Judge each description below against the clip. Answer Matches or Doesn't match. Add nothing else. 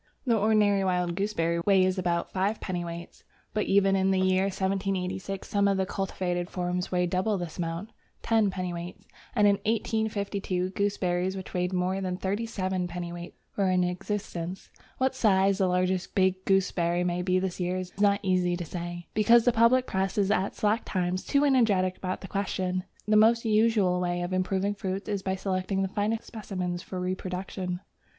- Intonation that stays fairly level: Matches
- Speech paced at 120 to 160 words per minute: Doesn't match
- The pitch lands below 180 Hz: Doesn't match